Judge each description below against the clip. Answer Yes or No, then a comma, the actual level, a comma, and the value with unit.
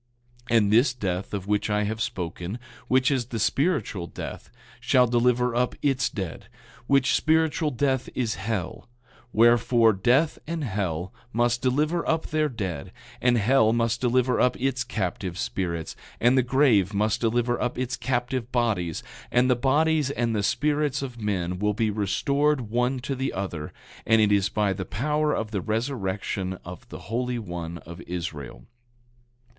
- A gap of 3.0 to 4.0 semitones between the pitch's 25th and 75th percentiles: No, average, 4.5 semitones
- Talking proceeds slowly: No, average, 160 wpm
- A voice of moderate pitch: No, low, 115 Hz